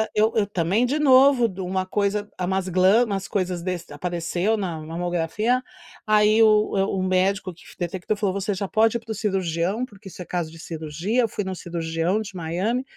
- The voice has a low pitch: No, high, 190 Hz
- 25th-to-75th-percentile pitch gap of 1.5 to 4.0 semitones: Yes, average, 3.4 semitones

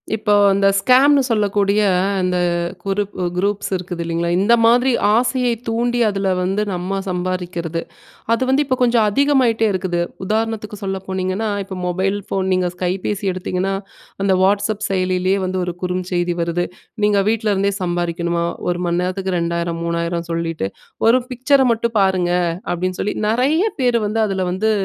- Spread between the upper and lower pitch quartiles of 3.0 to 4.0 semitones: Yes, average, 3.6 semitones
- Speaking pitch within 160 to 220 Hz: Yes, high, 195 Hz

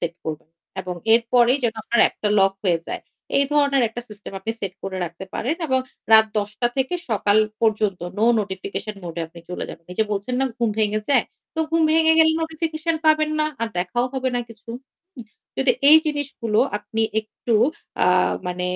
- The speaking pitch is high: Yes, high, 225 Hz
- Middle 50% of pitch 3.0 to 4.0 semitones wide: No, wide, 5.5 semitones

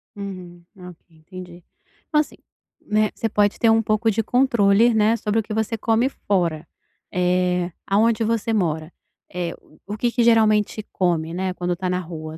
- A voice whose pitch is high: Yes, high, 200 Hz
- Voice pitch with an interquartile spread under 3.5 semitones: No, average, 3.9 semitones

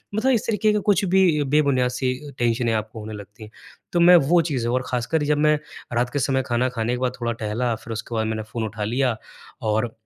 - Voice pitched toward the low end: Yes, low, 125 Hz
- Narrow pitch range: No, average, 4.9 semitones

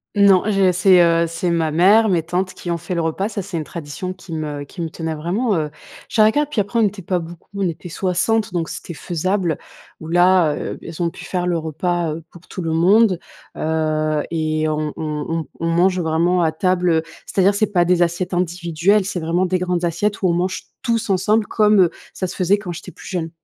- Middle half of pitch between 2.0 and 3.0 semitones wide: Yes, average, 2.7 semitones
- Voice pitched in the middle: Yes, medium, 175 Hz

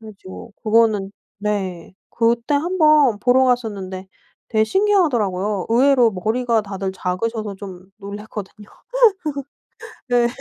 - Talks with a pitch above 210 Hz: Yes, high, 220 Hz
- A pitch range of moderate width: Yes, average, 3.8 semitones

